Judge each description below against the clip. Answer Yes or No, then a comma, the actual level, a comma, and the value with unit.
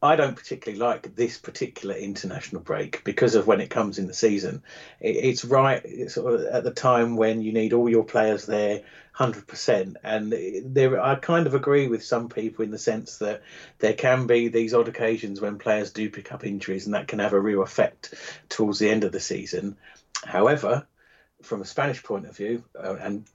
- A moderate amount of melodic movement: Yes, average, 3.1 semitones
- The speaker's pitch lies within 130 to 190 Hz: No, low, 110 Hz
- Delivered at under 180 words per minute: No, average, 195 wpm